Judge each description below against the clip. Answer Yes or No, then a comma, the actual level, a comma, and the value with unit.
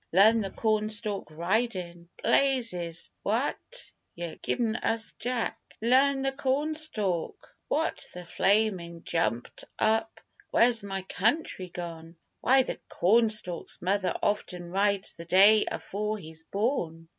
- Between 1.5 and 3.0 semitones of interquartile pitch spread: No, average, 4.9 semitones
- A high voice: Yes, high, 205 Hz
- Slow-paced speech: Yes, slow, 115 wpm